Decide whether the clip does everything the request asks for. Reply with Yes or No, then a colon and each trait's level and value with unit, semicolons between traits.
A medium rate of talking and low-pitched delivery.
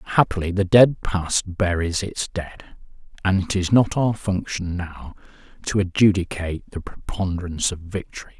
Yes: average, 145 wpm; very low, 95 Hz